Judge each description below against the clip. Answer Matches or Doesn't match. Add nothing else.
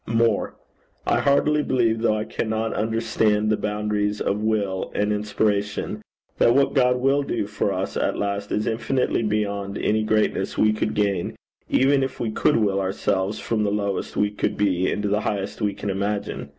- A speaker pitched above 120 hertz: Doesn't match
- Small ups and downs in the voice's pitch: Matches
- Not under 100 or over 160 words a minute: Doesn't match